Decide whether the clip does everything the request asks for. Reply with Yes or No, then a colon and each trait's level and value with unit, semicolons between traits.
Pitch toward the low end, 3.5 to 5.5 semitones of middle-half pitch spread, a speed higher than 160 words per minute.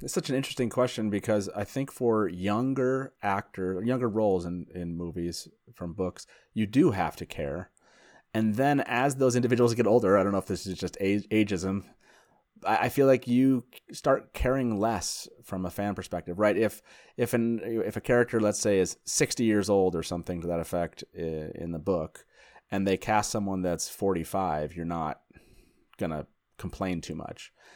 Yes: low, 105 Hz; average, 4.9 semitones; average, 180 wpm